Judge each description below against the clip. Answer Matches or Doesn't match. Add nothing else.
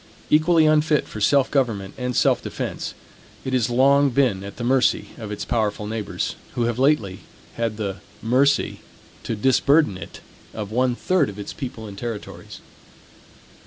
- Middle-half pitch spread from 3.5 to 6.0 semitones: Matches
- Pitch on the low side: Matches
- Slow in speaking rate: Doesn't match